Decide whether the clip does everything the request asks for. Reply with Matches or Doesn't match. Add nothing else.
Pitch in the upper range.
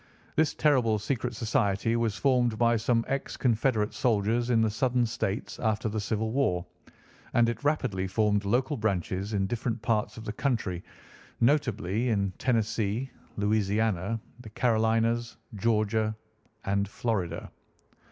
Doesn't match